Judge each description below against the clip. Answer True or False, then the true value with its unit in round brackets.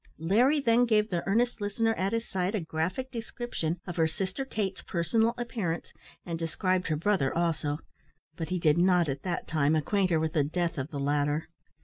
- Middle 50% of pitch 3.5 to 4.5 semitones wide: False (5.0 semitones)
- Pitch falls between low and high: True (180 Hz)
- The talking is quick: False (195 wpm)